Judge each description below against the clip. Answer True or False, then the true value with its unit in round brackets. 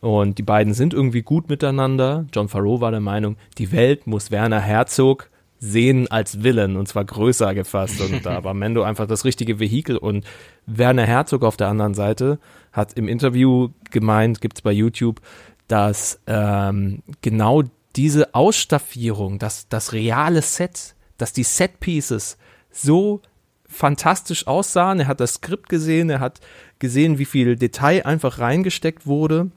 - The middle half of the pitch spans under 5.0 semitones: False (5.3 semitones)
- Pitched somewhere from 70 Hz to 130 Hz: True (120 Hz)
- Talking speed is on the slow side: False (155 wpm)